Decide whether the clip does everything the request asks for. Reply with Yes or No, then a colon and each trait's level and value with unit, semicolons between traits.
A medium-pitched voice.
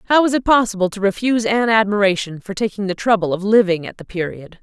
No: high, 205 Hz